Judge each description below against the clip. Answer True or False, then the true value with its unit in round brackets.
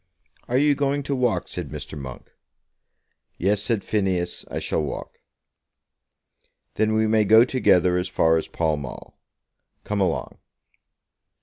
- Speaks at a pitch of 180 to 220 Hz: False (100 Hz)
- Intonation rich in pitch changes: True (5.7 semitones)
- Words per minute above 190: False (135 wpm)